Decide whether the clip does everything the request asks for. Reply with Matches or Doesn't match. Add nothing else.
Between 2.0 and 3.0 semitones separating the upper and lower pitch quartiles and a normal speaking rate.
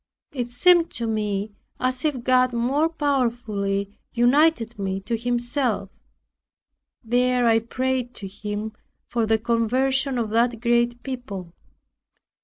Doesn't match